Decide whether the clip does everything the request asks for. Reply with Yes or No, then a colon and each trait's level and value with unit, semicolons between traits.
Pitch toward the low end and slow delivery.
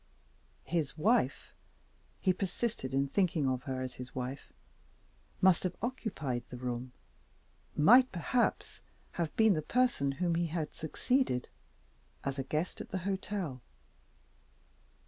No: medium, 160 Hz; slow, 125 wpm